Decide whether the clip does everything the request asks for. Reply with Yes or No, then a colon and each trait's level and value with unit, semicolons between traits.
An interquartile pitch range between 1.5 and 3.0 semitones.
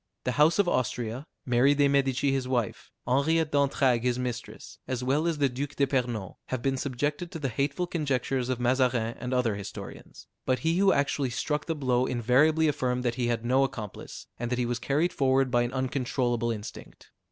Yes: average, 2.7 semitones